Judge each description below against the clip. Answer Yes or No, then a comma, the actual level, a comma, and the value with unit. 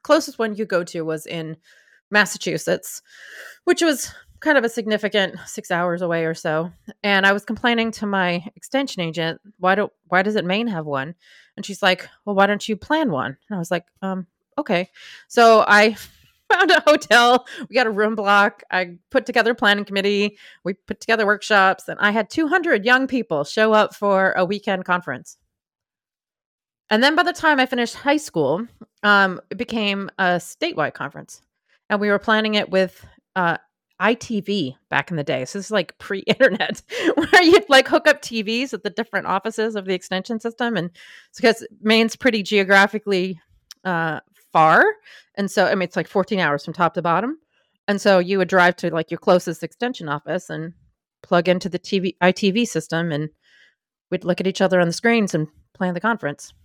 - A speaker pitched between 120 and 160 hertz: No, high, 200 Hz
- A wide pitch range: No, average, 4.2 semitones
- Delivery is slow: No, average, 190 wpm